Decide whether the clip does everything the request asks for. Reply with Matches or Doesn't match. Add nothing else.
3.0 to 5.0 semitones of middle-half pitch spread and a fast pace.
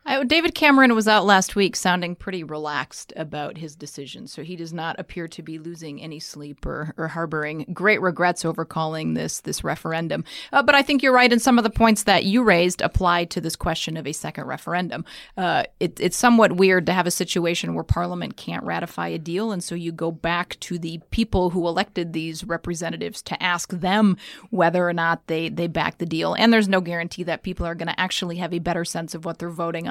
Doesn't match